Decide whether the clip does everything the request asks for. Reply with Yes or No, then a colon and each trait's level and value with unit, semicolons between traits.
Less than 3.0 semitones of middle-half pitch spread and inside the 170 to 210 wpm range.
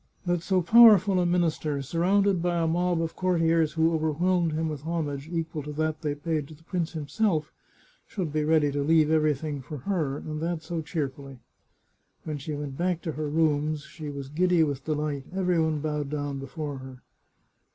Yes: narrow, 2.6 semitones; average, 195 wpm